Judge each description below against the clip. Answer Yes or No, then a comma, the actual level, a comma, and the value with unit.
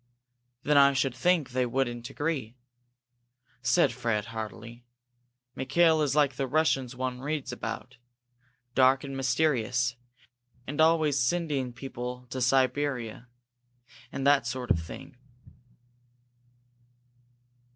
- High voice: No, low, 130 Hz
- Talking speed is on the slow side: Yes, slow, 110 wpm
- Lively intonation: No, average, 2.8 semitones